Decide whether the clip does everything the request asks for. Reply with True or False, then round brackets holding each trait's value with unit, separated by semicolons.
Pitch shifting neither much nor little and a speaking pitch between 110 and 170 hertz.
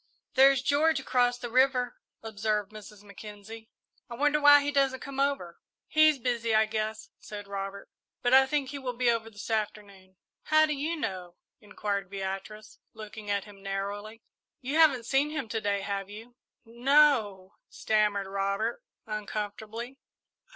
False (4.6 semitones; 220 Hz)